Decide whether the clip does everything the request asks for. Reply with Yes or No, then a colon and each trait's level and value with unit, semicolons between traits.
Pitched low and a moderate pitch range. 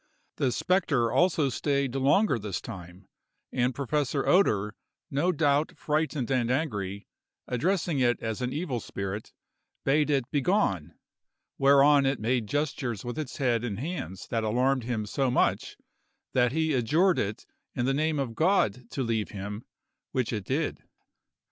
Yes: low, 130 Hz; average, 4.6 semitones